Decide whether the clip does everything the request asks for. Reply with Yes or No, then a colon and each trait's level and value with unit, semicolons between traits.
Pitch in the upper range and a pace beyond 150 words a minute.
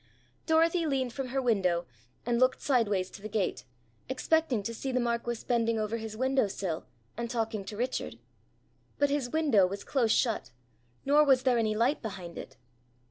Yes: high, 235 Hz; average, 175 wpm